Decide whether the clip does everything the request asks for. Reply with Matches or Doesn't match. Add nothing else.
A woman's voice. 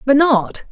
Matches